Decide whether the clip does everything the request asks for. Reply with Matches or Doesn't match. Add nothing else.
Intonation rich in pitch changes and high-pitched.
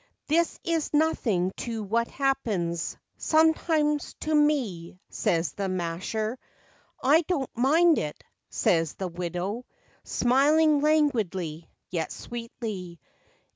Matches